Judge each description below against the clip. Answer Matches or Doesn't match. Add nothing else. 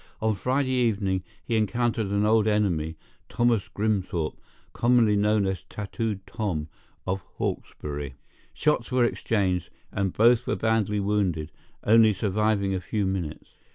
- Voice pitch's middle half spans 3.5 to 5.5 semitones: Doesn't match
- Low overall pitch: Matches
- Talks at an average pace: Doesn't match